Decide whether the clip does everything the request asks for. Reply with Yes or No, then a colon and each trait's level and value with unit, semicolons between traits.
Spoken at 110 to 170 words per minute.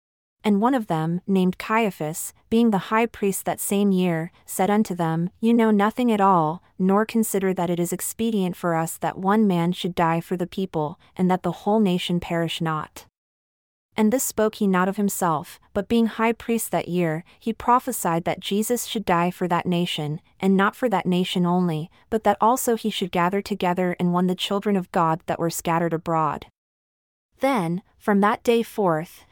No: average, 190 wpm